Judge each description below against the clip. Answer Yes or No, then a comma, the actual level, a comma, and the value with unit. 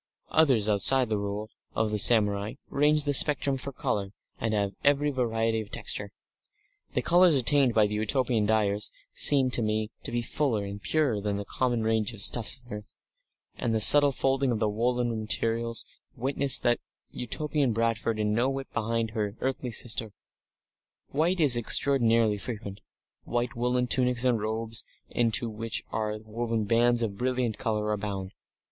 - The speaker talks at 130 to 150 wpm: No, average, 165 wpm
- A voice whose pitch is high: No, low, 115 Hz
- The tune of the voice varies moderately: Yes, average, 3.1 semitones